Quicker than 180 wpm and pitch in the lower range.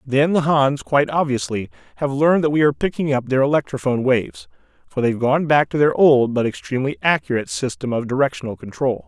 Yes: average, 190 wpm; low, 130 Hz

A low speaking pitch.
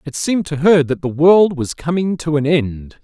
No: medium, 155 Hz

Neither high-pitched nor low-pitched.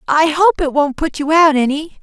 No: very high, 305 Hz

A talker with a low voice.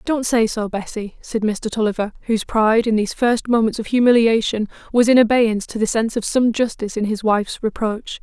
No: high, 225 Hz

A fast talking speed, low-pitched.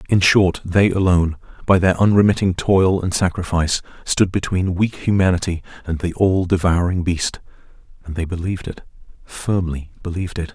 No: average, 150 wpm; very low, 90 Hz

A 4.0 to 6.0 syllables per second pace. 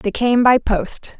No: 3.5 syllables/s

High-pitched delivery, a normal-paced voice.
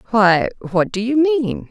Yes: high, 220 Hz; average, 175 wpm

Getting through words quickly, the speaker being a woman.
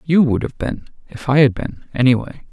No: fast, 240 wpm; male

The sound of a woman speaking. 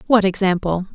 Yes: female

